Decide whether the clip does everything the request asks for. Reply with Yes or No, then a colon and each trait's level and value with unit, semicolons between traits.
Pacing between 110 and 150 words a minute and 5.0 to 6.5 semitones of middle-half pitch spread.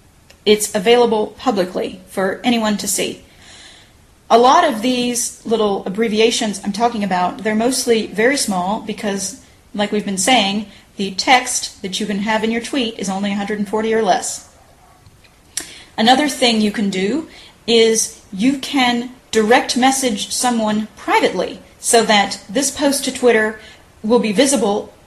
No: average, 145 wpm; average, 3.2 semitones